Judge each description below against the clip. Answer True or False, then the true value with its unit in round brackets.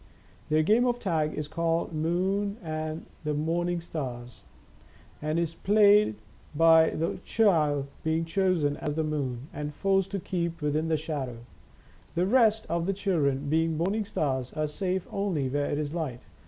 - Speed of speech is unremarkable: True (170 wpm)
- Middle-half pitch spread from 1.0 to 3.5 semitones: False (3.9 semitones)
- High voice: False (160 Hz)